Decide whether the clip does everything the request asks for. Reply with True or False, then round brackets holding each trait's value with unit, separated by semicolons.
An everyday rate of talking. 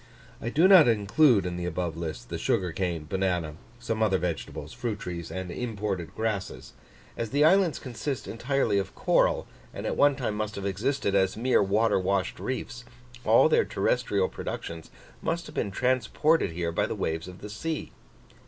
True (175 wpm)